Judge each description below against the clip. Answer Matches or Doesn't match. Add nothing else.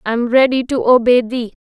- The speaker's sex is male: Doesn't match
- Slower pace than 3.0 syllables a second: Doesn't match